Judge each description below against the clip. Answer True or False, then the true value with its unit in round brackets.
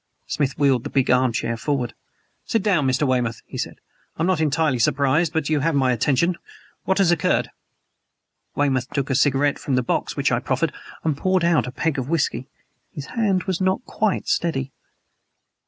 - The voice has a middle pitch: True (145 Hz)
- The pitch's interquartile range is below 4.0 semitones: False (4.4 semitones)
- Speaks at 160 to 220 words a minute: True (190 wpm)